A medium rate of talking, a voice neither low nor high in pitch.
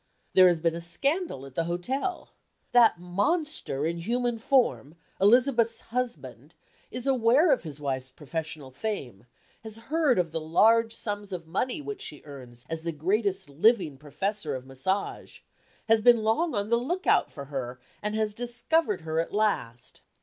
No: average, 160 wpm; high, 205 Hz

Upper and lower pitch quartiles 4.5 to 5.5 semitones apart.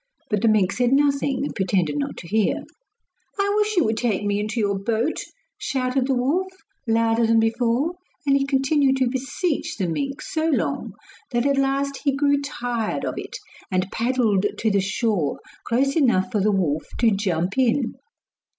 Yes: average, 4.9 semitones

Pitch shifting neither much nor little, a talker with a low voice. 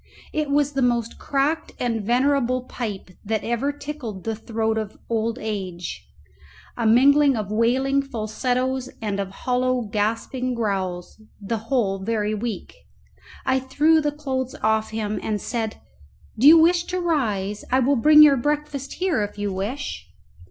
No: average, 4.3 semitones; high, 240 Hz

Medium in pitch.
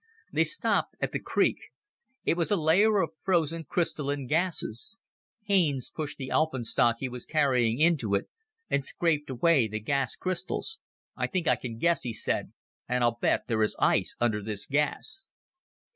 Yes: medium, 145 Hz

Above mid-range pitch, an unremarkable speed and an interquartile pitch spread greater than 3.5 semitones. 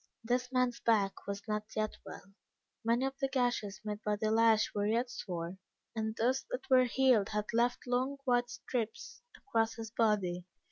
No: high, 225 Hz; average, 175 wpm; average, 2.8 semitones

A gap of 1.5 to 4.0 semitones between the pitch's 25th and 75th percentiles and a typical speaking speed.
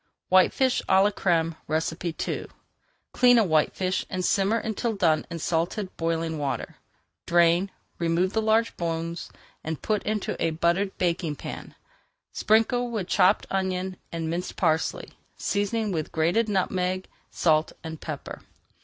No: average, 3.7 semitones; slow, 130 wpm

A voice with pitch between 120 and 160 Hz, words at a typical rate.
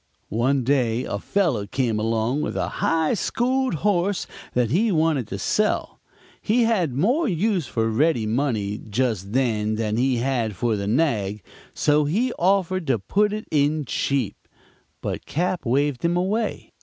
Yes: medium, 140 Hz; average, 155 wpm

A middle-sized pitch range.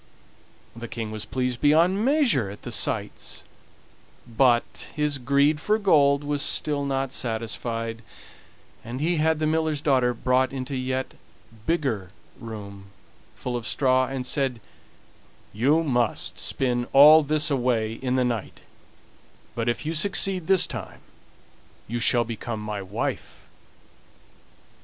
Yes: average, 4.1 semitones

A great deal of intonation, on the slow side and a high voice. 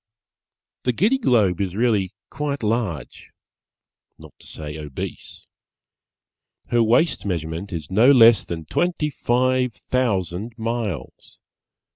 No: wide, 6.0 semitones; slow, 110 wpm; low, 110 Hz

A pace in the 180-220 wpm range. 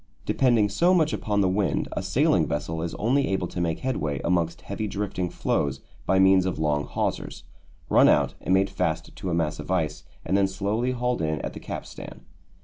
Yes: average, 200 wpm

